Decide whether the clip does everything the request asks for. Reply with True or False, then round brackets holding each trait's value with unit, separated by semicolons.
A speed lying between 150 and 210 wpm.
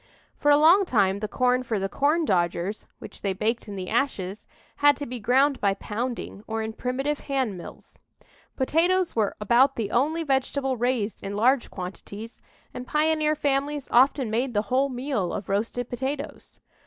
True (165 wpm)